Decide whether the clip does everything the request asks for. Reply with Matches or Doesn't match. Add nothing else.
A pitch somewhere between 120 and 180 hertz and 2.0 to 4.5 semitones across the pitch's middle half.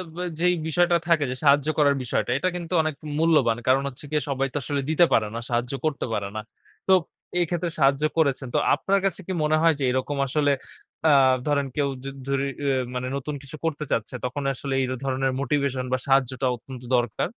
Matches